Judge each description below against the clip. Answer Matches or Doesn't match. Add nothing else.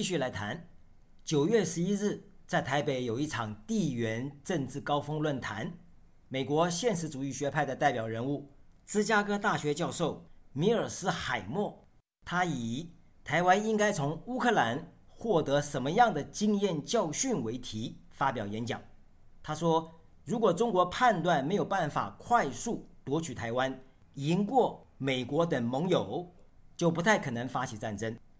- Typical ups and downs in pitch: Doesn't match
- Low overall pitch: Doesn't match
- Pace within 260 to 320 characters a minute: Doesn't match